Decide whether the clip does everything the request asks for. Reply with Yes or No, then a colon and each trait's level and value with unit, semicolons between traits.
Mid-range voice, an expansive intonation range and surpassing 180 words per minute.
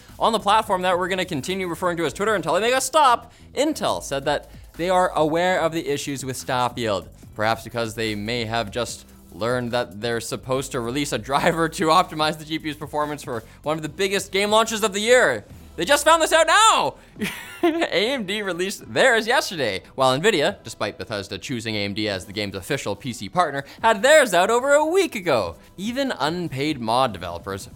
Yes: medium, 155 Hz; wide, 9.0 semitones; average, 195 wpm